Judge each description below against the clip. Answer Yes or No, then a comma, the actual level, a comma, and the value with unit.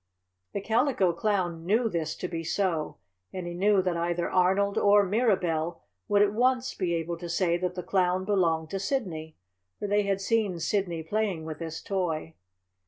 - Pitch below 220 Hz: Yes, medium, 185 Hz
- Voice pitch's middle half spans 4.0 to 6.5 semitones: No, average, 3.3 semitones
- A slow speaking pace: No, average, 175 wpm